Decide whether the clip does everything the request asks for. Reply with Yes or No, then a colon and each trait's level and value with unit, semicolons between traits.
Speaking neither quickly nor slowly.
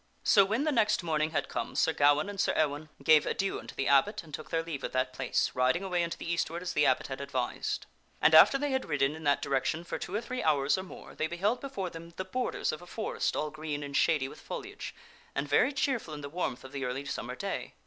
No: fast, 255 wpm